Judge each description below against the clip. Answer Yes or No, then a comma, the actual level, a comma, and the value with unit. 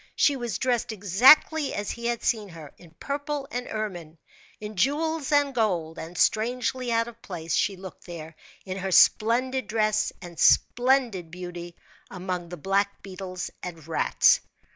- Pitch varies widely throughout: Yes, wide, 5.7 semitones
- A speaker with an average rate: Yes, average, 155 wpm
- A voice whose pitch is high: Yes, high, 210 Hz